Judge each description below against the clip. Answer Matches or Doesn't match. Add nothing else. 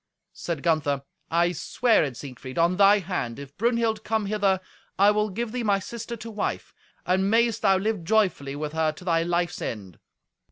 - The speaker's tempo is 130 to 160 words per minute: Doesn't match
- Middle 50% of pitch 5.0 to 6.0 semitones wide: Matches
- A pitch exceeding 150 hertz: Matches